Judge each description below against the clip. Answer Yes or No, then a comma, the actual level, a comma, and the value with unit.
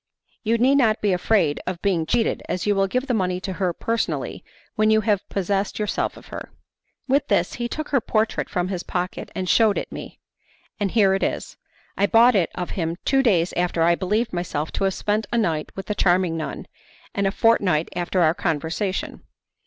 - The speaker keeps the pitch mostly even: No, average, 3.7 semitones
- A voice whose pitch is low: No, high, 195 Hz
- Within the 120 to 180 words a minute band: No, fast, 205 wpm